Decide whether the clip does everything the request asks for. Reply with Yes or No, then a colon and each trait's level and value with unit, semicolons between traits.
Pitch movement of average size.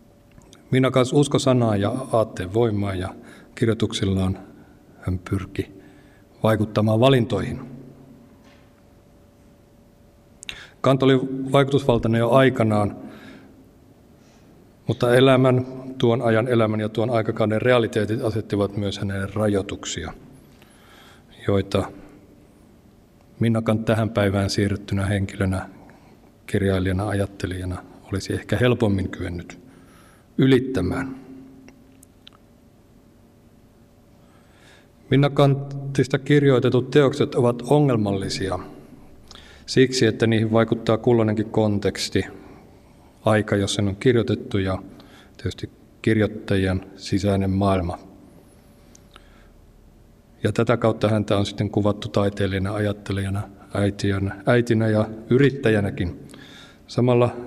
Yes: average, 3.6 semitones